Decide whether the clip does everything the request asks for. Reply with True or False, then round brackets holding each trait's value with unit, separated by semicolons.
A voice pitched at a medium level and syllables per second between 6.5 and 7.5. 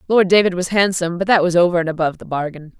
True (175 Hz; 7.3 syllables/s)